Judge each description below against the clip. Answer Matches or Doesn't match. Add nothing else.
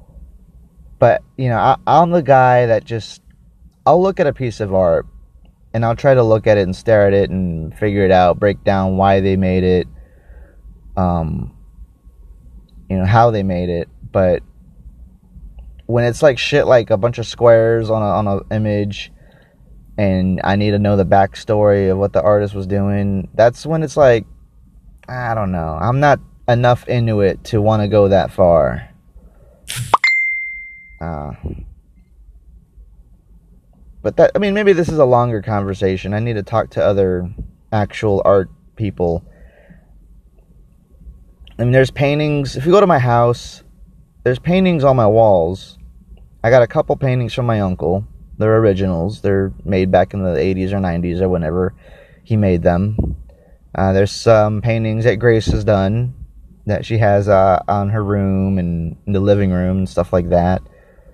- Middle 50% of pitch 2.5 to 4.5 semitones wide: Doesn't match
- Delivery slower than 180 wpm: Matches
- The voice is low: Matches